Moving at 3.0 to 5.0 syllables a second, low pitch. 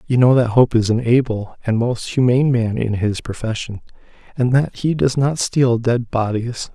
Yes: 4.7 syllables/s; low, 120 Hz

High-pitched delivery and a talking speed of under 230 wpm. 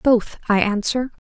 Yes: high, 225 Hz; average, 140 wpm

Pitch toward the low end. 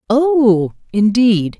No: high, 225 Hz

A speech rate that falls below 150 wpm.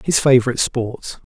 Yes: slow, 135 wpm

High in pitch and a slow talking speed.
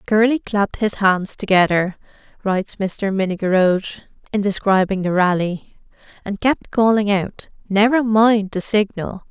Yes: high, 200 Hz; slow, 130 wpm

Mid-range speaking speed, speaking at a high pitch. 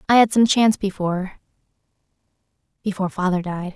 No: slow, 110 wpm; high, 195 Hz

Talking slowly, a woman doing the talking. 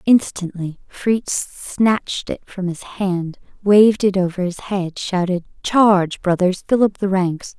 No: average, 150 wpm; female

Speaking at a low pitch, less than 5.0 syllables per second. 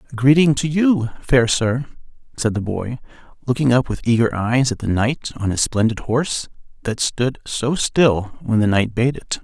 Yes: low, 125 Hz; 4.5 syllables/s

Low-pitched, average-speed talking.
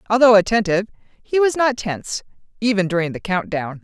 No: high, 210 Hz; average, 155 wpm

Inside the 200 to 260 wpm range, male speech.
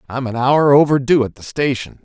Yes: fast, 205 wpm; male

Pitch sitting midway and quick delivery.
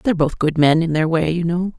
Yes: medium, 165 Hz; fast, 300 wpm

